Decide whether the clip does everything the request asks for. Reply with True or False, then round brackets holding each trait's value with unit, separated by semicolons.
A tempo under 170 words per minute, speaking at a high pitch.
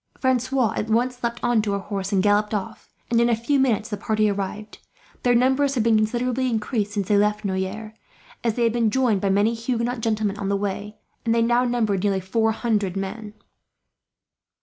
False (200 wpm; 220 Hz)